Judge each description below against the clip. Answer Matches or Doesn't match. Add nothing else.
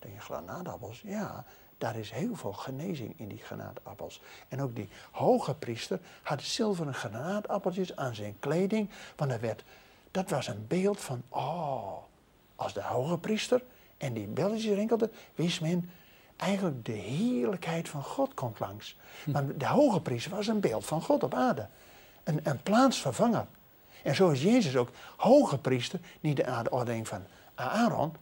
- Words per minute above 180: Doesn't match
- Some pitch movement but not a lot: Doesn't match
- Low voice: Doesn't match